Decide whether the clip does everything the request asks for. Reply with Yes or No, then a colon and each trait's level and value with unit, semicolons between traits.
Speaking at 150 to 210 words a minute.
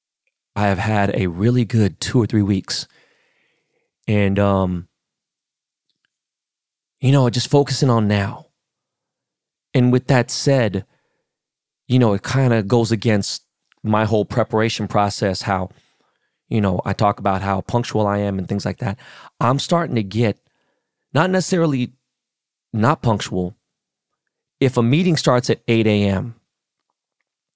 No: slow, 135 wpm